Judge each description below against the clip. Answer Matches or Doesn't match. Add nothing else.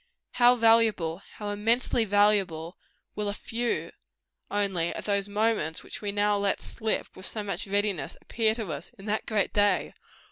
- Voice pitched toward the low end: Doesn't match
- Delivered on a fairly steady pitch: Matches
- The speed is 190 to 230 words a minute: Doesn't match